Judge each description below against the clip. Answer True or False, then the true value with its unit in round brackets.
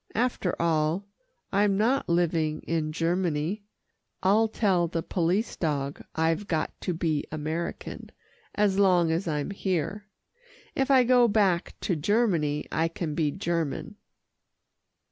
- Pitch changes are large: False (4.2 semitones)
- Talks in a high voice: False (175 Hz)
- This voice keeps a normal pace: False (125 wpm)